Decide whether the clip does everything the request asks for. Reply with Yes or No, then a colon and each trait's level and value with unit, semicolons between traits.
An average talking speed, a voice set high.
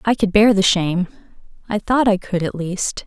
Yes: average, 195 wpm; high, 195 Hz